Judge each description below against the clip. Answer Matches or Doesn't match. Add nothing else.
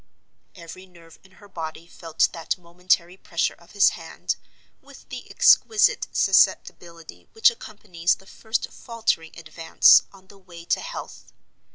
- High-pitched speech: Doesn't match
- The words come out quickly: Doesn't match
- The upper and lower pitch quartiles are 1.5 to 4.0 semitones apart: Matches